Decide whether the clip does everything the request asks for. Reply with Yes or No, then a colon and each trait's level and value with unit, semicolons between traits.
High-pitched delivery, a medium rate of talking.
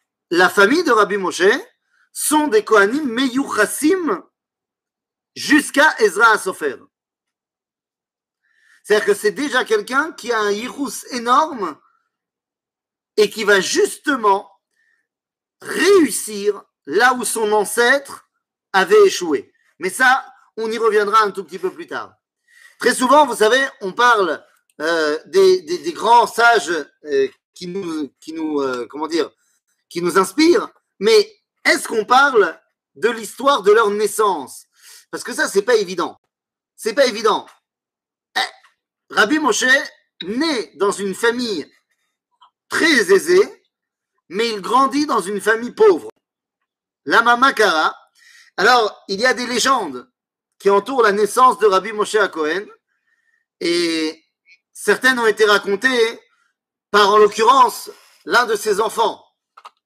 No: very high, 255 Hz; slow, 130 wpm